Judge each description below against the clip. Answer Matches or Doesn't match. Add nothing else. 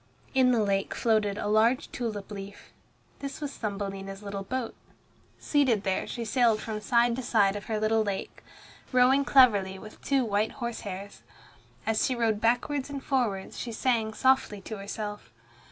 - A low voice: Doesn't match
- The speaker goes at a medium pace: Matches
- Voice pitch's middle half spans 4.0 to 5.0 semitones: Doesn't match